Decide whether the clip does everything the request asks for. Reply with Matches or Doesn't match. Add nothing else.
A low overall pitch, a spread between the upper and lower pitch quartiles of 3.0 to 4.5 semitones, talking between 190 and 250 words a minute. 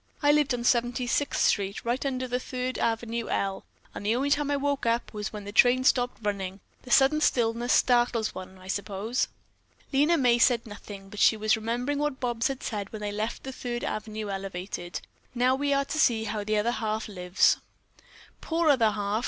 Doesn't match